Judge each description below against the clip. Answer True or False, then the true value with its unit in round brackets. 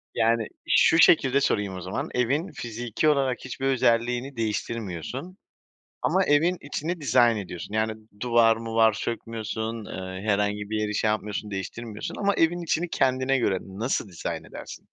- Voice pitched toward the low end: True (115 Hz)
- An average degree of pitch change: True (4.3 semitones)